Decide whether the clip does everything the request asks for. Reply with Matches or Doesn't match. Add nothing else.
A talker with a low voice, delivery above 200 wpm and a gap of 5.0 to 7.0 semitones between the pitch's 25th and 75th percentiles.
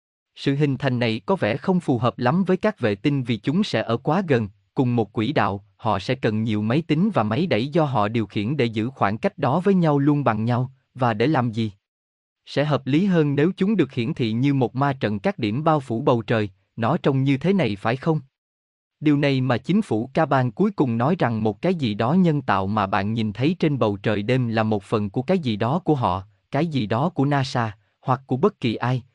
Matches